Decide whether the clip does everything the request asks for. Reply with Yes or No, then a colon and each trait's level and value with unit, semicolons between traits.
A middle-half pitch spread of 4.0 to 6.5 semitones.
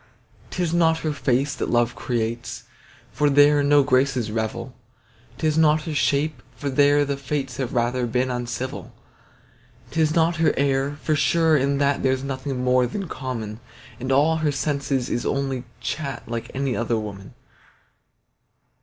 No: average, 3.0 semitones